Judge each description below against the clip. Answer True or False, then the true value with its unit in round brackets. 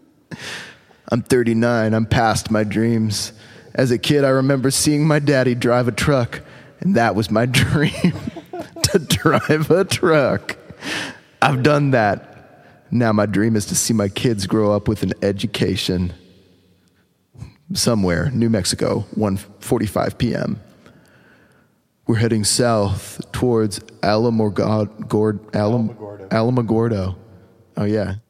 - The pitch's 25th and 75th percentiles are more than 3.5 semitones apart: False (3.1 semitones)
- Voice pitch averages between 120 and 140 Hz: False (110 Hz)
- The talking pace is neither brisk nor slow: False (115 wpm)